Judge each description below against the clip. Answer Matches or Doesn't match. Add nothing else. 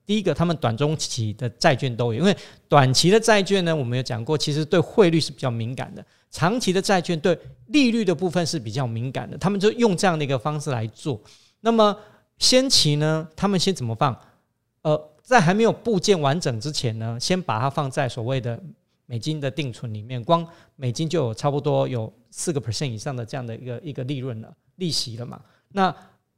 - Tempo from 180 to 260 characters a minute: Doesn't match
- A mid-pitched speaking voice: Matches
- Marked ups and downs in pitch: Matches